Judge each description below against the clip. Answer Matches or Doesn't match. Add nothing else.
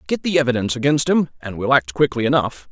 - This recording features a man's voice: Matches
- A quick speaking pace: Matches